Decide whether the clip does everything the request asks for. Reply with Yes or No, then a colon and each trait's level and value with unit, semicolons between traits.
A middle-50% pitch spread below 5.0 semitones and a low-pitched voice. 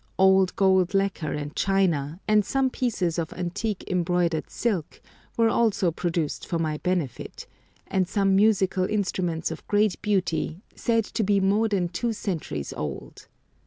No: average, 3.5 semitones; medium, 185 Hz